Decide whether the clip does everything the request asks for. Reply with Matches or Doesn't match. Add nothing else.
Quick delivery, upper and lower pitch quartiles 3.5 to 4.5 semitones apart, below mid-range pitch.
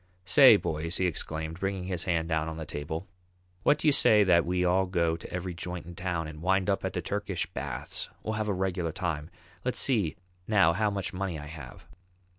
Doesn't match